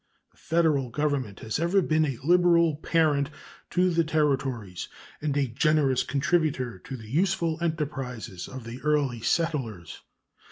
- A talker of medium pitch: Yes, medium, 145 Hz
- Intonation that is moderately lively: Yes, average, 4.3 semitones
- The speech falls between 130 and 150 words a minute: Yes, slow, 135 wpm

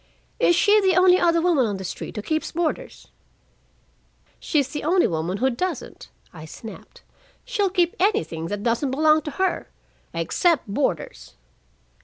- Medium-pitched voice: No, very high, 310 Hz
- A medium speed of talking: Yes, average, 150 wpm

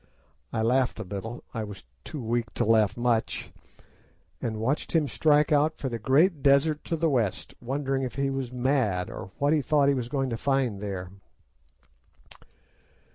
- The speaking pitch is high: No, low, 130 Hz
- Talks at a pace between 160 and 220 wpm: Yes, average, 165 wpm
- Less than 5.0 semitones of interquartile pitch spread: Yes, average, 4.0 semitones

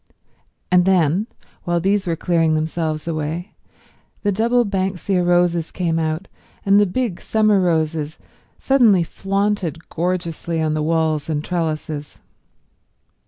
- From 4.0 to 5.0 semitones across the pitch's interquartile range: No, average, 3.4 semitones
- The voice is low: No, medium, 175 Hz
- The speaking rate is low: Yes, slow, 120 wpm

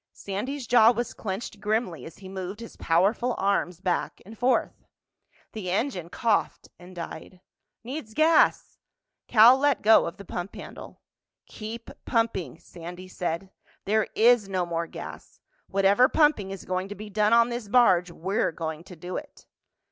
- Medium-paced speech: Yes, average, 155 wpm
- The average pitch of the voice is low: No, high, 200 Hz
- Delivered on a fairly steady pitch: No, average, 4.3 semitones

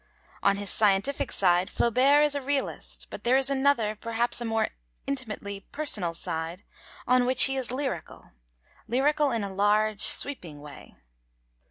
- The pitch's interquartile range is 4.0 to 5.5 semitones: Yes, average, 5.2 semitones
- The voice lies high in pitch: Yes, high, 235 Hz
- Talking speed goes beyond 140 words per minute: Yes, average, 150 wpm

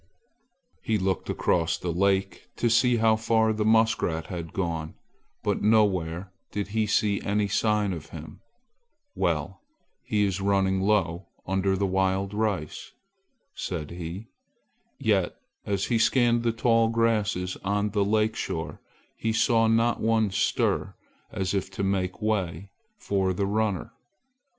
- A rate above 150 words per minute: No, average, 140 wpm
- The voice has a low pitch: Yes, low, 100 Hz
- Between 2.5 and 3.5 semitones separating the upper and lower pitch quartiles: Yes, average, 2.9 semitones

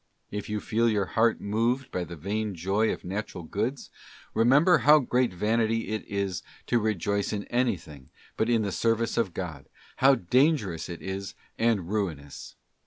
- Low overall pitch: Yes, low, 105 Hz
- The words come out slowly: No, average, 165 wpm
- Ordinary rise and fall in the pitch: Yes, average, 3.7 semitones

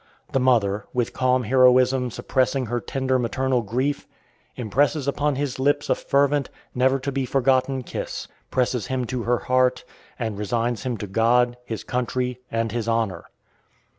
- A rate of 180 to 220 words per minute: No, average, 155 wpm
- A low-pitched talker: Yes, low, 125 Hz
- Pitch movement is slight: Yes, narrow, 2.2 semitones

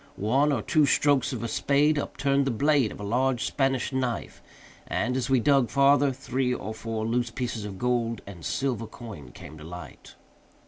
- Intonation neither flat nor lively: Yes, average, 3.6 semitones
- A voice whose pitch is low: Yes, low, 125 Hz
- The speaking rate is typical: Yes, average, 185 wpm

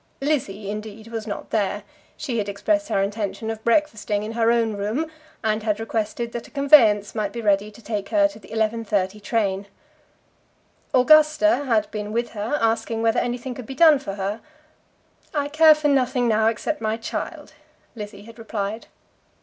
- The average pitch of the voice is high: Yes, high, 225 Hz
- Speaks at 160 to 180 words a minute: Yes, average, 175 wpm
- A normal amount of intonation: Yes, average, 3.2 semitones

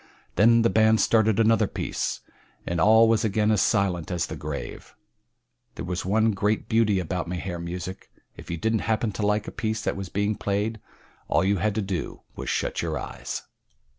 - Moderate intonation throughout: Yes, average, 3.3 semitones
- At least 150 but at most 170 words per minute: No, average, 190 wpm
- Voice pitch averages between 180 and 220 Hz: No, low, 105 Hz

